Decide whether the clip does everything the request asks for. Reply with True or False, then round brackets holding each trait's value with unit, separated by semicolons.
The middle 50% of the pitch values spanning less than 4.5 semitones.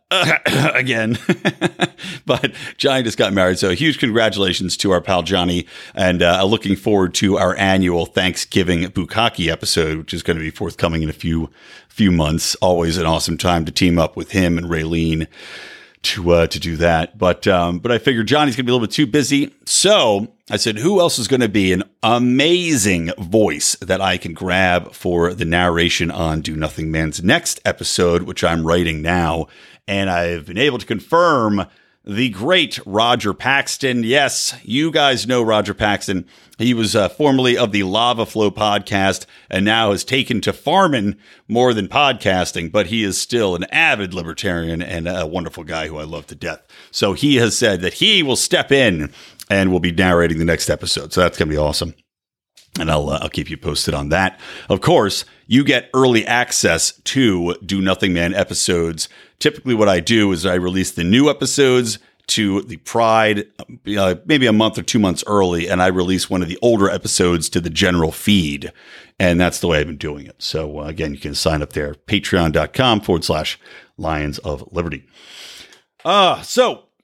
False (4.8 semitones)